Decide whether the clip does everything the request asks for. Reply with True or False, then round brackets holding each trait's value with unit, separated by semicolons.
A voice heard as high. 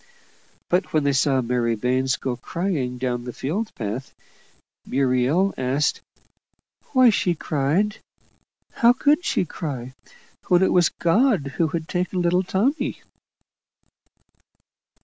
False (155 Hz)